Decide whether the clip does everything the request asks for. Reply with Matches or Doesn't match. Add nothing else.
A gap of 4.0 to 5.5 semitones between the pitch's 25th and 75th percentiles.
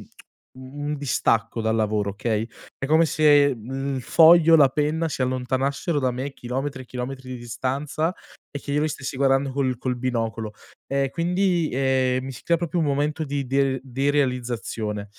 Doesn't match